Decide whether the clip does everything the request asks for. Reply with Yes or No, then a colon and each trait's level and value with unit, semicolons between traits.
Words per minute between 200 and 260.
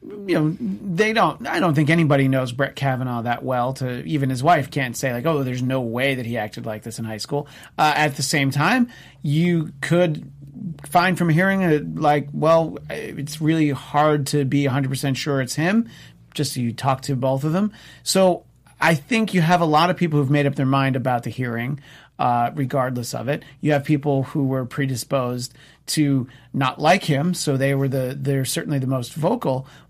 Yes: fast, 205 wpm